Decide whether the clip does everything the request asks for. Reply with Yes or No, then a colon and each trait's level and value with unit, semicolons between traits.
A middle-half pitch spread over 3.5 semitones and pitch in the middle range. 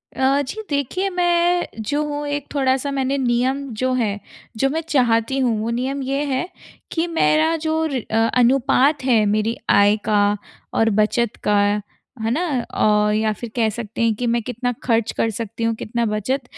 No: average, 4.0 semitones; very high, 250 Hz